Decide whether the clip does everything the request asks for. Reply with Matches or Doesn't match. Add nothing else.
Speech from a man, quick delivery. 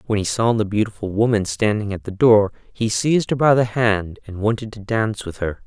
Matches